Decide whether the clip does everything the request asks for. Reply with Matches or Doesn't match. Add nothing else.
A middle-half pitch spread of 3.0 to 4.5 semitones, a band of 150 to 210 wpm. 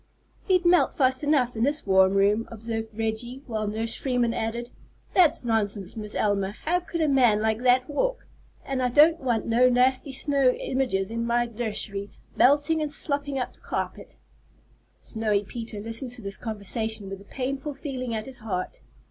Matches